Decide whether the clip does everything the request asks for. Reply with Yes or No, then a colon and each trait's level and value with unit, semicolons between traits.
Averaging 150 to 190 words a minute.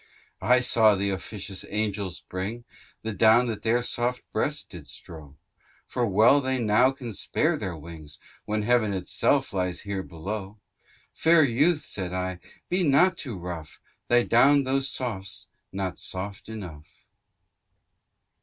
No: average, 140 wpm